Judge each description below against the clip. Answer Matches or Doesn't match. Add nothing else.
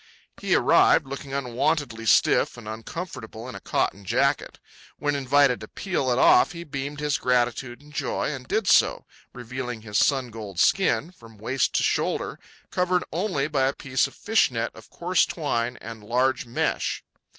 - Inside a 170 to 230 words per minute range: Matches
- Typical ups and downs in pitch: Matches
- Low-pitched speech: Matches